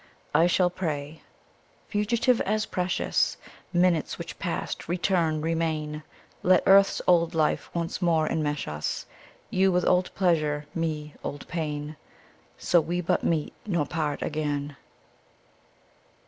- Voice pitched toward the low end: No, medium, 165 Hz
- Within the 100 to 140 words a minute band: Yes, slow, 135 wpm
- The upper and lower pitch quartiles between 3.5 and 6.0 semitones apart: No, average, 2.9 semitones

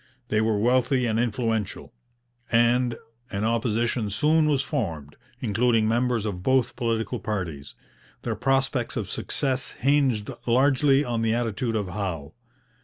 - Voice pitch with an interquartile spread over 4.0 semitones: No, average, 3.2 semitones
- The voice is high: No, low, 115 Hz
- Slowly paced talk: Yes, slow, 130 wpm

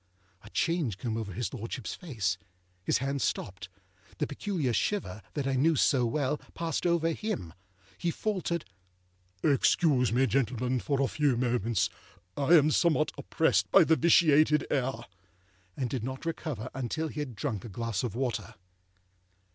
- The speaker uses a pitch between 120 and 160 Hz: Yes, low, 135 Hz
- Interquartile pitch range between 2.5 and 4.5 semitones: No, average, 5.0 semitones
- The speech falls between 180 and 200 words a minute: No, average, 155 wpm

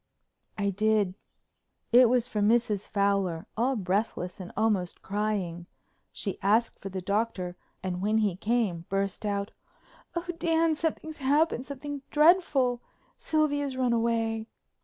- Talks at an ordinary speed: No, slow, 125 wpm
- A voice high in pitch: Yes, high, 220 Hz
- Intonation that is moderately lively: Yes, average, 4.6 semitones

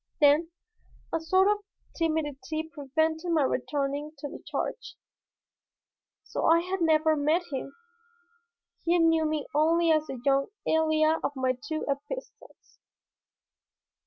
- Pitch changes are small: Yes, narrow, 2.2 semitones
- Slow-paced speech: Yes, slow, 125 wpm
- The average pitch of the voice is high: Yes, very high, 315 Hz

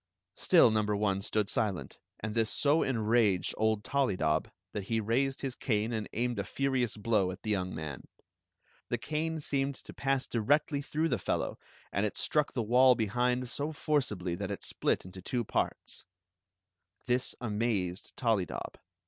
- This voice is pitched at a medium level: No, low, 115 Hz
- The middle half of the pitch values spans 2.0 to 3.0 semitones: No, average, 4.4 semitones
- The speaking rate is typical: Yes, average, 160 wpm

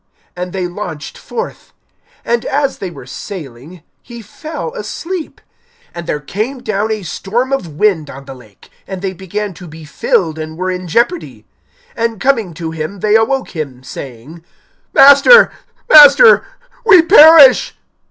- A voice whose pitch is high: Yes, high, 195 Hz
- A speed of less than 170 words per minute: Yes, average, 150 wpm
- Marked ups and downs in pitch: Yes, wide, 8.8 semitones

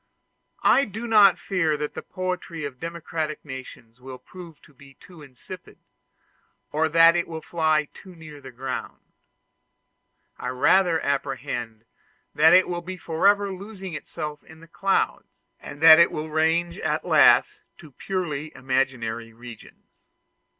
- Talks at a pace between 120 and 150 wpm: Yes, slow, 135 wpm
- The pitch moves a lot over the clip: No, average, 4.6 semitones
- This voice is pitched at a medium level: Yes, medium, 160 Hz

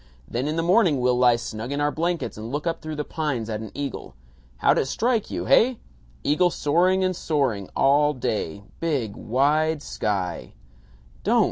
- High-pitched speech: No, medium, 145 Hz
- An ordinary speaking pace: Yes, average, 180 wpm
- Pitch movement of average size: No, wide, 5.9 semitones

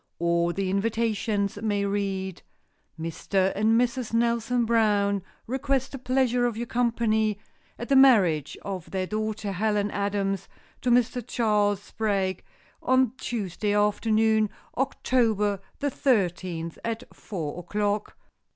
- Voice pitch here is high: Yes, high, 210 Hz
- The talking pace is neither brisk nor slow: No, slow, 120 wpm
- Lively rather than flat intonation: No, average, 3.0 semitones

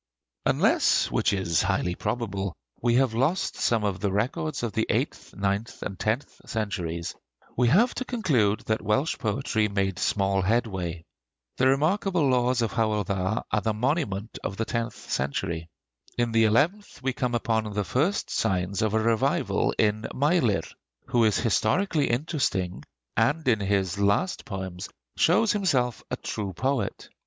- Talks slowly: No, average, 155 wpm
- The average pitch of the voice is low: Yes, low, 110 Hz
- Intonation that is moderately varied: Yes, average, 4.6 semitones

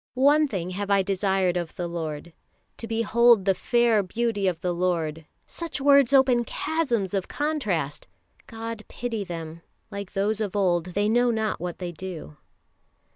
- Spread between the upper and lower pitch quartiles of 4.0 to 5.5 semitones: Yes, average, 5.0 semitones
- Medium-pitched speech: No, high, 200 Hz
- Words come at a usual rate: Yes, average, 160 wpm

